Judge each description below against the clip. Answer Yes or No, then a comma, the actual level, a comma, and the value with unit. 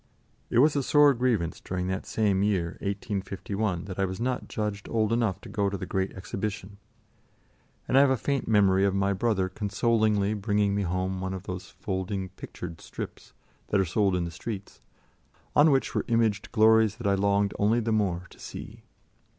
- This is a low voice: Yes, low, 100 Hz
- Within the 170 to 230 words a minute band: Yes, average, 190 wpm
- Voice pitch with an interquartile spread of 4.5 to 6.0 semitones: No, average, 2.8 semitones